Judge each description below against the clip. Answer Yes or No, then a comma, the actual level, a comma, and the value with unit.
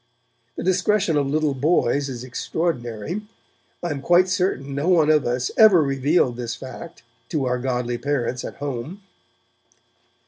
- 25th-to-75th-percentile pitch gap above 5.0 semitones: Yes, wide, 5.5 semitones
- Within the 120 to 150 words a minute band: Yes, average, 145 wpm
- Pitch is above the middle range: No, medium, 140 Hz